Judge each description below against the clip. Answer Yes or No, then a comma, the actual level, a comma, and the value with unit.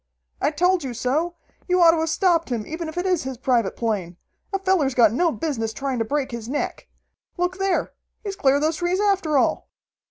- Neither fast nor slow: No, fast, 210 wpm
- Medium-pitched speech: No, very high, 310 Hz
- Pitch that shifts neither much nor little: No, wide, 5.9 semitones